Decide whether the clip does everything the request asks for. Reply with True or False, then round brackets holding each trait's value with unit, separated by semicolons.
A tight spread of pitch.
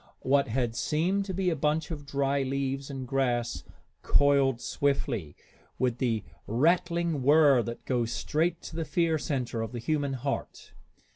False (3.9 semitones)